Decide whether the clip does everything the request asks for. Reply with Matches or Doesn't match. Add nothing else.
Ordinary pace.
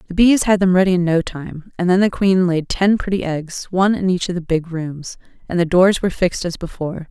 Doesn't match